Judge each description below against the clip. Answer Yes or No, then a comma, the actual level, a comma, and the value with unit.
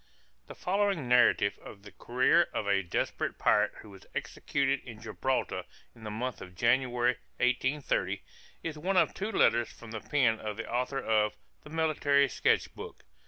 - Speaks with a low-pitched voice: Yes, low, 125 Hz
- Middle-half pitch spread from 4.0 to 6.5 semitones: Yes, average, 4.4 semitones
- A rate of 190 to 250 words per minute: No, average, 165 wpm